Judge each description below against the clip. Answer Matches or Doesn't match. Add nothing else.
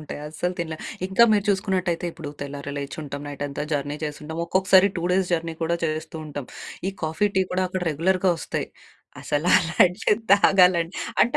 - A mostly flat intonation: Doesn't match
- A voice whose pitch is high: Doesn't match